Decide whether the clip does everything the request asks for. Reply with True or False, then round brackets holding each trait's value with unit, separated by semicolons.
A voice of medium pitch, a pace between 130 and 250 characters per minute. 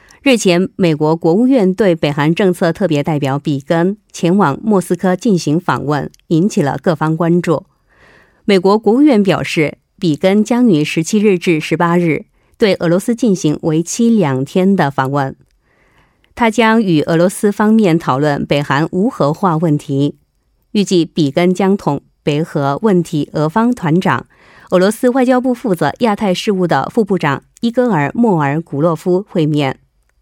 True (175 Hz; 240 characters per minute)